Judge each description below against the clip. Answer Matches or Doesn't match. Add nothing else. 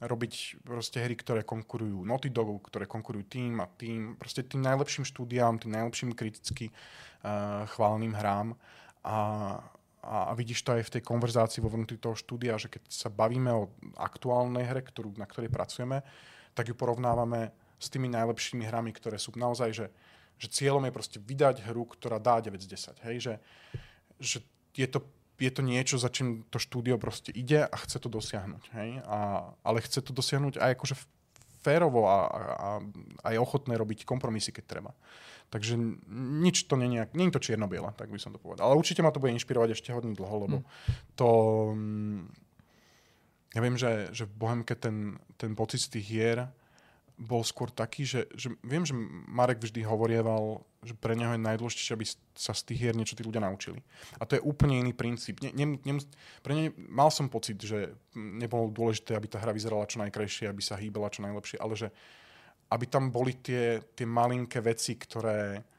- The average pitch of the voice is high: Doesn't match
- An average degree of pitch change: Doesn't match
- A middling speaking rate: Doesn't match